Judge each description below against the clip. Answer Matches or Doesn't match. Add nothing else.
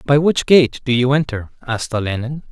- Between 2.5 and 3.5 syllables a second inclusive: Doesn't match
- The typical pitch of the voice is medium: Doesn't match